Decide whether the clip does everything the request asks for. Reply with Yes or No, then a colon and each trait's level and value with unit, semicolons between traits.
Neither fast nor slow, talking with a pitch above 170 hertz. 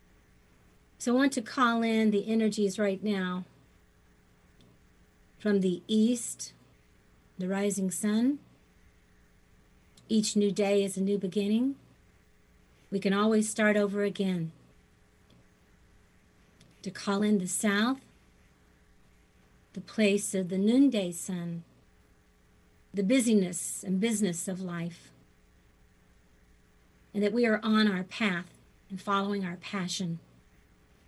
No: slow, 110 wpm; medium, 185 Hz